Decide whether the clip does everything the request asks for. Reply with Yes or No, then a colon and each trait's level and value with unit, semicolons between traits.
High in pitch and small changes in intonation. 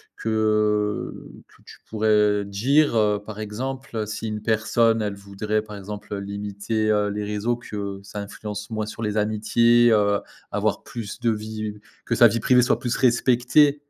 No: low, 110 Hz; narrow, 1.9 semitones